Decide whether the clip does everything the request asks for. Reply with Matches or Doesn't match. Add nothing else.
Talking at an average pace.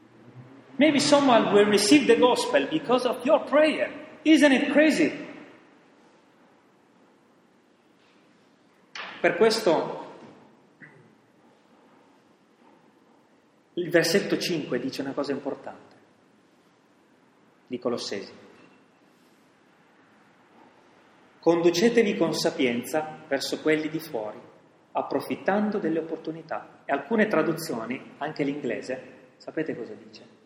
Doesn't match